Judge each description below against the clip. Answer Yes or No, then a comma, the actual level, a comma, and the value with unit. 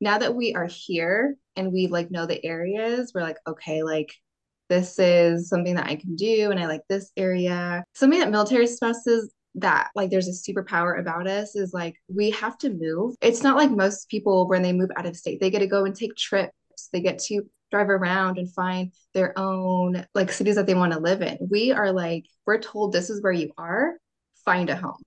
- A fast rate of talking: Yes, fast, 220 wpm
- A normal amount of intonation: Yes, average, 3.1 semitones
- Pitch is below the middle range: No, high, 190 Hz